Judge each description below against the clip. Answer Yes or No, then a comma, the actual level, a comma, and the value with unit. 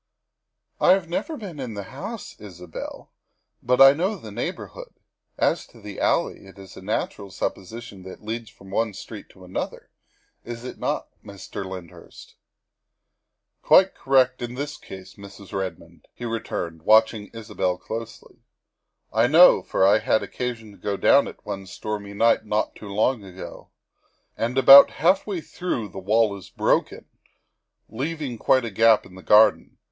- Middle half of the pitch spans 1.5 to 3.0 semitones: No, average, 4.5 semitones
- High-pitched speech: No, low, 110 Hz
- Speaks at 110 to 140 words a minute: No, average, 170 wpm